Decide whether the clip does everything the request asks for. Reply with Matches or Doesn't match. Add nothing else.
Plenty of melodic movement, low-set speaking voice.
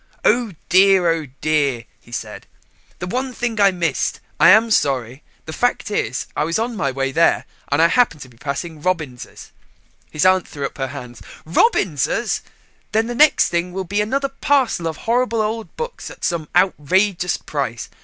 Doesn't match